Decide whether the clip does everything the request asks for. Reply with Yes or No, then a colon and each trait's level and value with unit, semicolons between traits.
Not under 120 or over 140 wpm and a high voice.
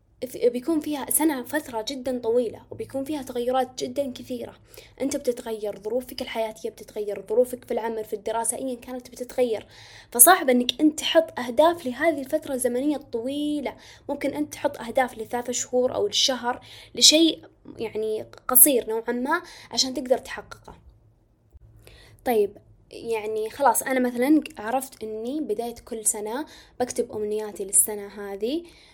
Yes: average, 130 wpm; very high, 250 Hz